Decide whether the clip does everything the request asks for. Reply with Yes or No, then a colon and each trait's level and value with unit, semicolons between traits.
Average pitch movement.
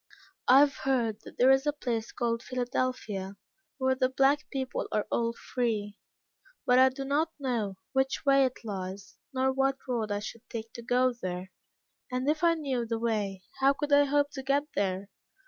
Yes: average, 3.6 semitones